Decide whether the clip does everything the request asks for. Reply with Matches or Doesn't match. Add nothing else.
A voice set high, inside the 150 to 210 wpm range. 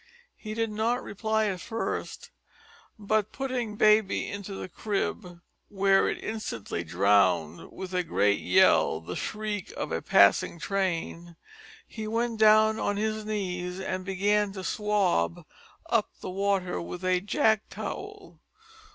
Doesn't match